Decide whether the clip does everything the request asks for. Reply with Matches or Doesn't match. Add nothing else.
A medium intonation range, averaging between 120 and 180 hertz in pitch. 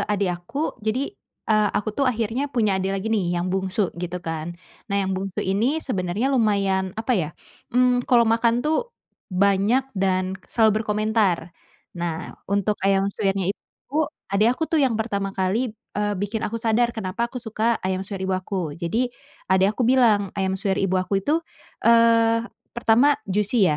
Doesn't match